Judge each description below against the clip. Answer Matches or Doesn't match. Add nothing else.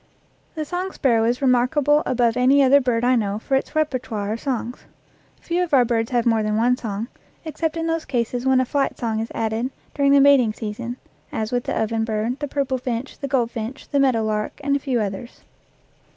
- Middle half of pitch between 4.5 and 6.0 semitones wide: Doesn't match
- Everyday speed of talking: Doesn't match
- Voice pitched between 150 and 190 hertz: Doesn't match